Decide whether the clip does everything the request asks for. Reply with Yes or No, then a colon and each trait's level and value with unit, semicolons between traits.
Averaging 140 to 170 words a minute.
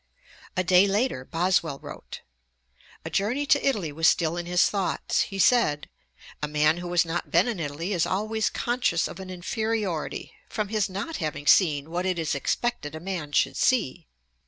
No: average, 195 wpm